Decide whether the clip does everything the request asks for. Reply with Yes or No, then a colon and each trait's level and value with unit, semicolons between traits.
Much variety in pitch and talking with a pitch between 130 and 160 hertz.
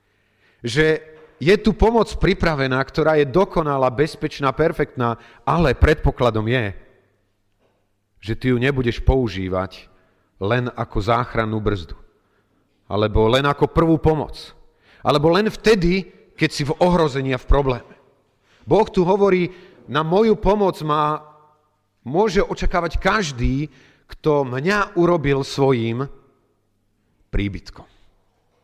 Yes: wide, 6.6 semitones; low, 135 Hz